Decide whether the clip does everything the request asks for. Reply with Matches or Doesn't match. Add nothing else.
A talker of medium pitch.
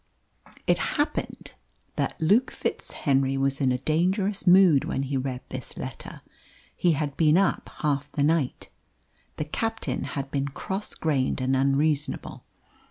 Matches